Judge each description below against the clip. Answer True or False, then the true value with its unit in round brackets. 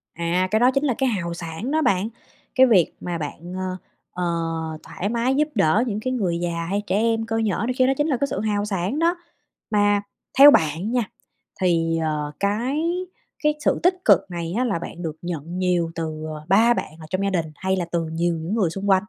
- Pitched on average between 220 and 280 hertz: False (190 Hz)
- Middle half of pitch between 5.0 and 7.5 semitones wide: True (5.5 semitones)